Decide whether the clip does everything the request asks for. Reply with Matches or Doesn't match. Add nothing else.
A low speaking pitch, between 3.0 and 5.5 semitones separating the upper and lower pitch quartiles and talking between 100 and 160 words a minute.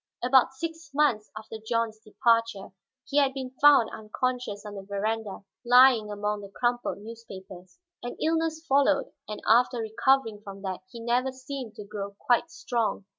Doesn't match